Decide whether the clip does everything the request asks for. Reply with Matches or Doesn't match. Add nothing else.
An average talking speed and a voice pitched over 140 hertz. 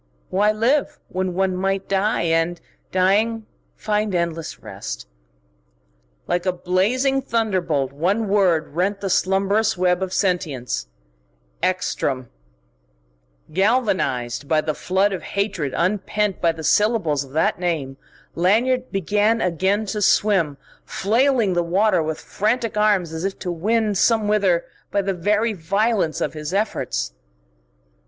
Doesn't match